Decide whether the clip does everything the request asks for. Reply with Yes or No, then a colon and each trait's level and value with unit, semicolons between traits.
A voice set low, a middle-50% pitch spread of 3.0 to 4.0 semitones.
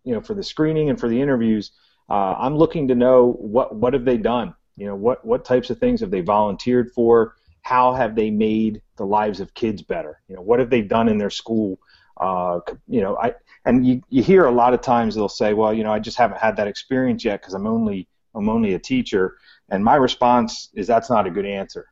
Yes: low, 120 Hz; average, 3.7 semitones